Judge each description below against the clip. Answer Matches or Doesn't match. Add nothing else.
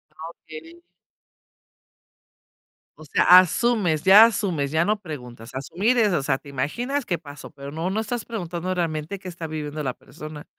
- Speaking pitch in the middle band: Matches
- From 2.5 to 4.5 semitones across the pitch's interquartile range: Doesn't match